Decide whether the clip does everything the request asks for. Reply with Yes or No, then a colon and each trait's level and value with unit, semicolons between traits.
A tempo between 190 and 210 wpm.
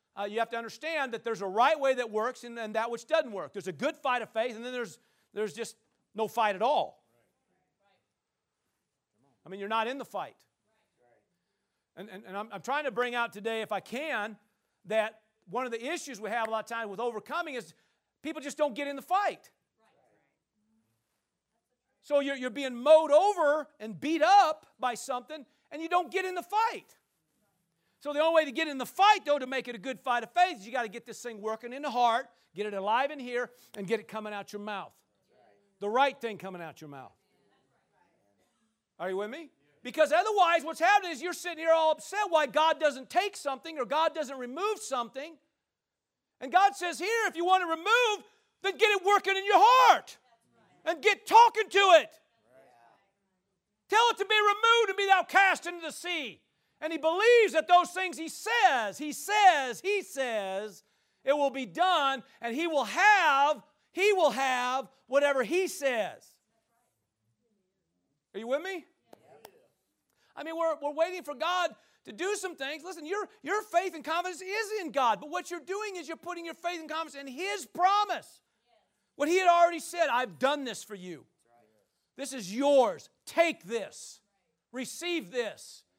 Yes: average, 195 wpm